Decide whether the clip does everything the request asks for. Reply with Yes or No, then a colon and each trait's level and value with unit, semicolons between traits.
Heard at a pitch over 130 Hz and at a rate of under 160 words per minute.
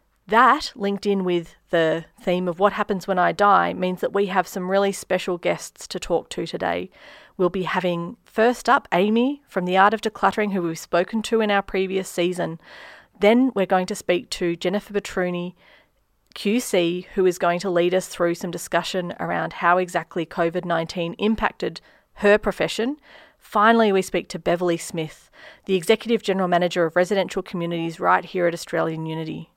No: medium, 185 Hz; average, 175 wpm